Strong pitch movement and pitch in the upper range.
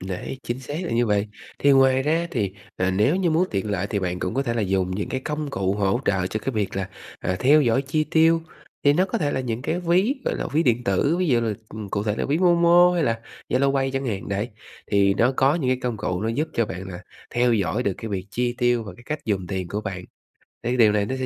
No: wide, 5.9 semitones; low, 120 Hz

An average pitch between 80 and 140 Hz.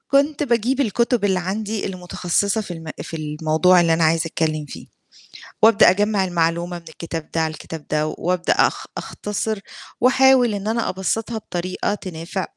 No: medium, 185 Hz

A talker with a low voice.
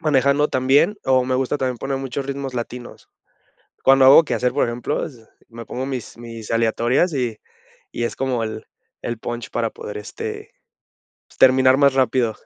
Yes: low, 130 Hz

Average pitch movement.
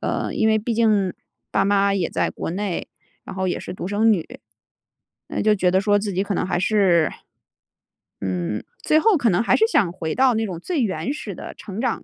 Yes: average, 3.5 semitones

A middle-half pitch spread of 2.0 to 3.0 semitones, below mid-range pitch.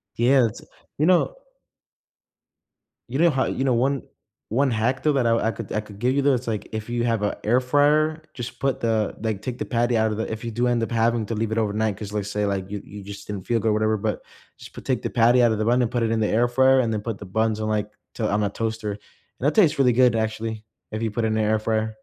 Yes: narrow, 2.4 semitones; low, 115 Hz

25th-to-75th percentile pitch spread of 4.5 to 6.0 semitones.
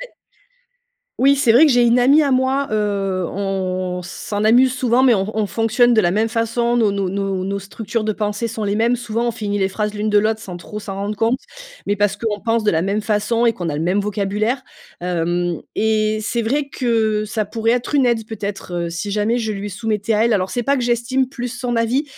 No: average, 3.0 semitones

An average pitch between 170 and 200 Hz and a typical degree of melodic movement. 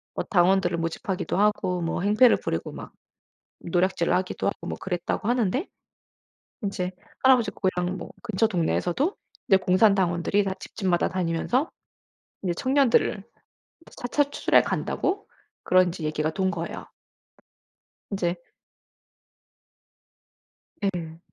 Yes: high, 190 Hz; average, 3.4 semitones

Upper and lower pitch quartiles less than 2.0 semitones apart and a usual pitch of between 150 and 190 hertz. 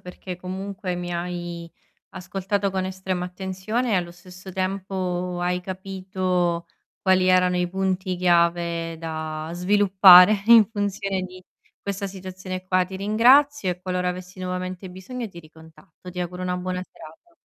Yes: narrow, 1.3 semitones; medium, 185 Hz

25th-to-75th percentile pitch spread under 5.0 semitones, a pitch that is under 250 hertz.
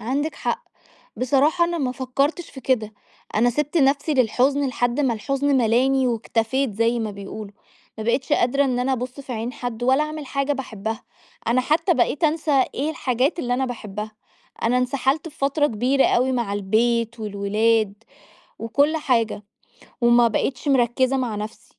No: average, 3.3 semitones; very high, 255 Hz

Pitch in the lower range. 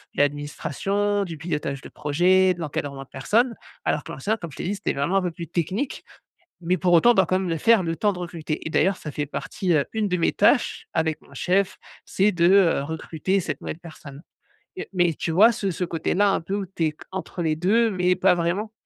No: medium, 175 Hz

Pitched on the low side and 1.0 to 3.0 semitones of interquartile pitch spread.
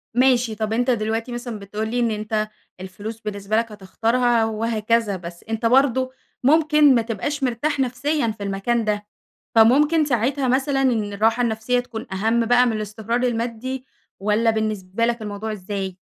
No: high, 230 Hz; average, 2.7 semitones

